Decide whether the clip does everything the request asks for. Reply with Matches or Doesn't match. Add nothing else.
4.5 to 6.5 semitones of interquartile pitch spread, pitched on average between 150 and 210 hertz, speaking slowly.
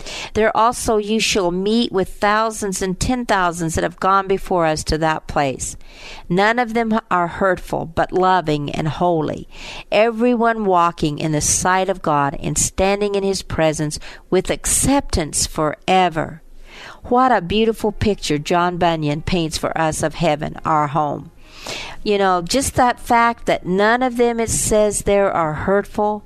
Doesn't match